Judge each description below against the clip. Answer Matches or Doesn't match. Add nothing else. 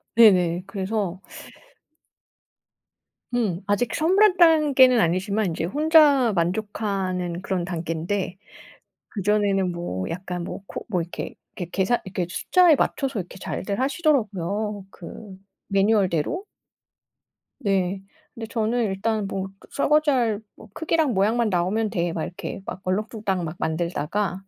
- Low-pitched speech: Doesn't match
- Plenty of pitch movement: Doesn't match